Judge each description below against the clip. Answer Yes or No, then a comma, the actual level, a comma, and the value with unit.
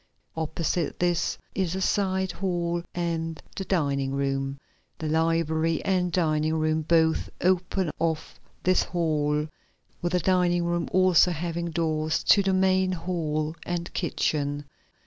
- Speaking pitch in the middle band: Yes, medium, 170 Hz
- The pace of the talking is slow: Yes, slow, 130 wpm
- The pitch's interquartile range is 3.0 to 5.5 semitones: No, narrow, 2.4 semitones